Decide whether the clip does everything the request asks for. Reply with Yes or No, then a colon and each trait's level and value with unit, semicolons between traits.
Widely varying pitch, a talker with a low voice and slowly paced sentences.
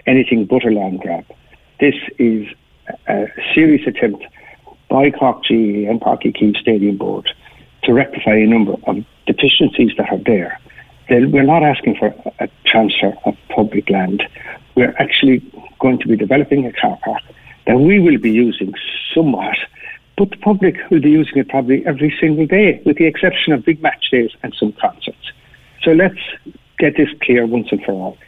No: wide, 5.8 semitones; low, 130 Hz; average, 170 wpm